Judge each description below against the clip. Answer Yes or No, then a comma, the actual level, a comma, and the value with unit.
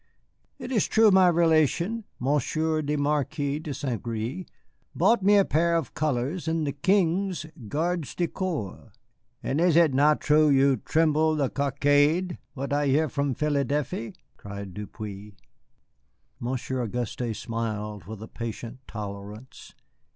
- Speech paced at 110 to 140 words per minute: Yes, slow, 135 wpm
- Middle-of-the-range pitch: Yes, medium, 145 Hz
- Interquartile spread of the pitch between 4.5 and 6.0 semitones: Yes, average, 5.3 semitones